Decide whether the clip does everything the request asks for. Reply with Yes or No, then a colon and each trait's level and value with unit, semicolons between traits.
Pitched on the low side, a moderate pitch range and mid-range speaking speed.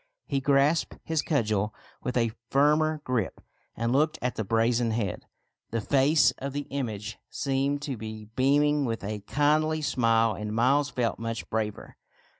Yes: low, 125 Hz; average, 4.3 semitones; average, 155 wpm